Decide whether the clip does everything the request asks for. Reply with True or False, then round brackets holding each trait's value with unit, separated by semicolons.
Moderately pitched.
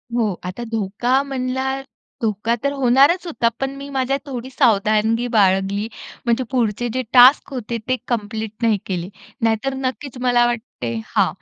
False (240 Hz)